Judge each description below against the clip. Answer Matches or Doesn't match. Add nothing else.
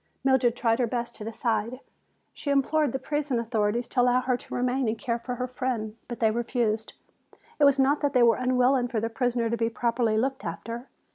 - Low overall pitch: Doesn't match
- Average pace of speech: Doesn't match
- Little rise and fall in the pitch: Matches